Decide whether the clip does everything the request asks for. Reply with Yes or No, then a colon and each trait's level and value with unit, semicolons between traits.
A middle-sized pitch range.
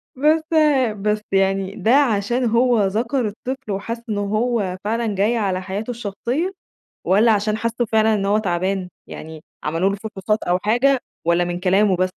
Yes: average, 3.3 semitones